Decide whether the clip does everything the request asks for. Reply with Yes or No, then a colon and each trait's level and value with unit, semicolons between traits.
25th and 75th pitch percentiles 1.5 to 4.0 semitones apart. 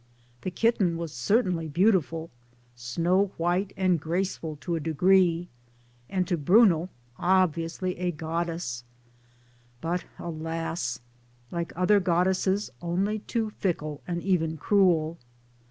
Yes: narrow, 2.5 semitones